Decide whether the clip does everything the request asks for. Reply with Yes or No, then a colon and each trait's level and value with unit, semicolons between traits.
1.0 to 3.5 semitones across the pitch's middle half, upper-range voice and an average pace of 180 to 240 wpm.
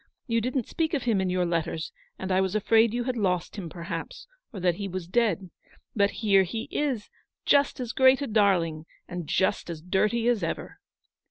No: average, 4.7 semitones; high, 200 Hz; average, 195 wpm